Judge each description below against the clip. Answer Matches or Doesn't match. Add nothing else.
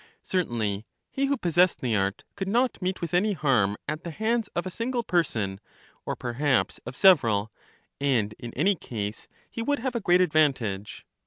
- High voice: Doesn't match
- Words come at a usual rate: Matches